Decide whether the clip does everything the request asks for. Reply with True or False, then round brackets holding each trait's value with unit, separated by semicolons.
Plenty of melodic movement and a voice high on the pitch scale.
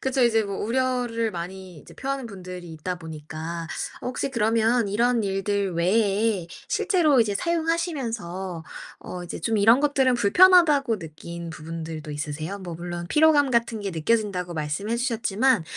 True (6.2 semitones; 205 Hz)